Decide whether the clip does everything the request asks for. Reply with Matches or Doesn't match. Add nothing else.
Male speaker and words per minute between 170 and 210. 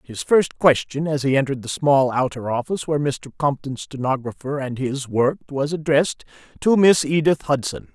Matches